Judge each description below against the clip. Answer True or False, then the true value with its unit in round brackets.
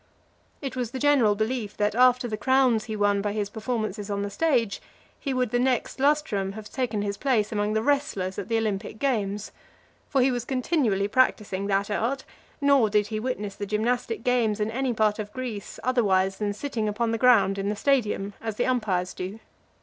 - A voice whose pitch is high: True (220 Hz)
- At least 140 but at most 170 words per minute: False (195 wpm)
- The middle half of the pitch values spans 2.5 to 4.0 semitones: True (3.6 semitones)